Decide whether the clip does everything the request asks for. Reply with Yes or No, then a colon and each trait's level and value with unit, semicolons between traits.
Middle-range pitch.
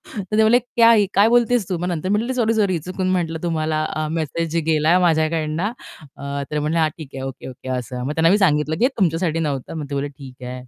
Yes: medium, 165 Hz